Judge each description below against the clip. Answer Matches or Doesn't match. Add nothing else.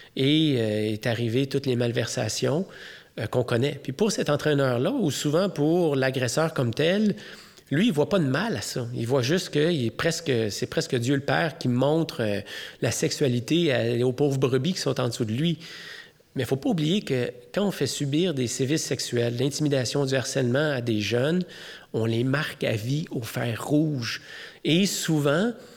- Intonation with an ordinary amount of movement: Matches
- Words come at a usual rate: Matches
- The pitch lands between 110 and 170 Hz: Matches